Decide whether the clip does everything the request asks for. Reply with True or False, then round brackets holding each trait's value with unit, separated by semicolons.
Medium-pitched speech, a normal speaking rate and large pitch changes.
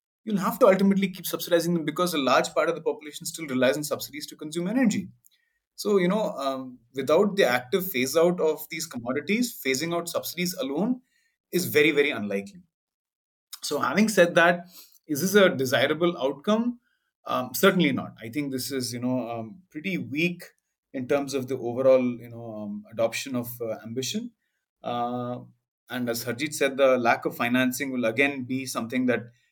True (150 Hz; 175 wpm; 6.1 semitones)